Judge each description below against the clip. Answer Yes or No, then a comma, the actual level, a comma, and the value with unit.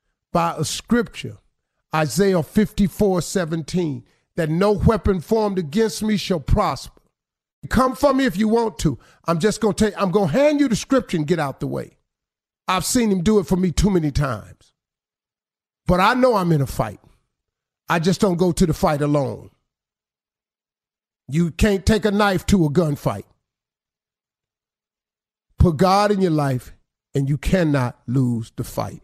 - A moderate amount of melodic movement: No, wide, 5.8 semitones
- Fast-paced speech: No, average, 165 wpm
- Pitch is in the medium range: Yes, medium, 180 Hz